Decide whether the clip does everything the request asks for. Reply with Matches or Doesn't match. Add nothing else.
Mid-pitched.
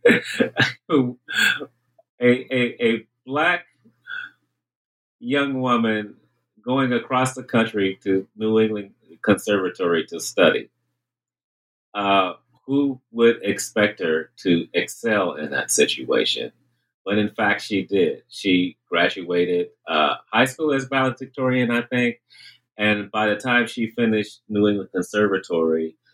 Doesn't match